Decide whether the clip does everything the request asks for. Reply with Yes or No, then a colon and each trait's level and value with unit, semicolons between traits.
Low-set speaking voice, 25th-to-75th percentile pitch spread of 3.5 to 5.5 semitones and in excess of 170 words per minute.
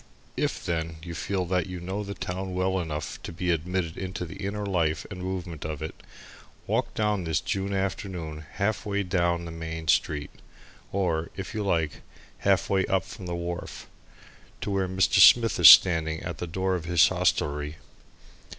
No: very low, 90 Hz; average, 2.8 semitones; average, 180 wpm